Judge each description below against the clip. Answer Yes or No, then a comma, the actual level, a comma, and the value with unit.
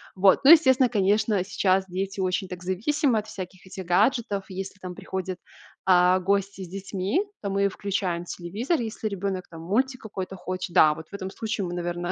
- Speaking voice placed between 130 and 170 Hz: No, high, 190 Hz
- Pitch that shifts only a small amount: Yes, narrow, 2.2 semitones